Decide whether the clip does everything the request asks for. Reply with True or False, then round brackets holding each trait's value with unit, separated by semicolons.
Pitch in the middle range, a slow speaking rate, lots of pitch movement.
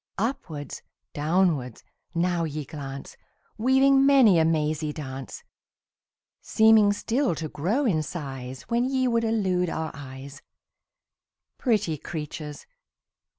True (165 Hz; 110 wpm; 7.3 semitones)